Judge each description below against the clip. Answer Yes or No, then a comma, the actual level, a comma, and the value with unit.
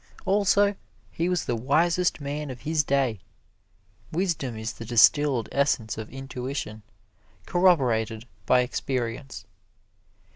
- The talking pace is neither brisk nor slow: No, slow, 110 wpm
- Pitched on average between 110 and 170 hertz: Yes, low, 135 Hz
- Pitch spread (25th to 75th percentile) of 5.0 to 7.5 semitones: Yes, average, 5.3 semitones